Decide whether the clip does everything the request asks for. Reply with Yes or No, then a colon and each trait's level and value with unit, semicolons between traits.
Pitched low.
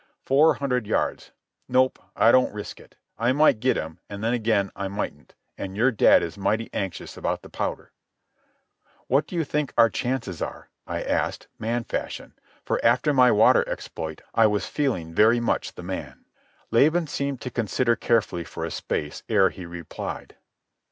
Yes: low, 115 Hz